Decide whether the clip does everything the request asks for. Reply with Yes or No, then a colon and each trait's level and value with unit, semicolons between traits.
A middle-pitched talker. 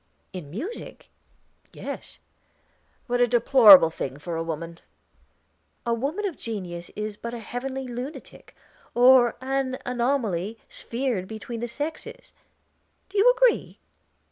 No: high, 240 Hz